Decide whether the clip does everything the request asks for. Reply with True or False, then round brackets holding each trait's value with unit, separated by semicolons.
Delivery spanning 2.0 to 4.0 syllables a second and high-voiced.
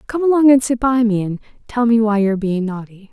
False (6.0 syllables/s; 225 Hz)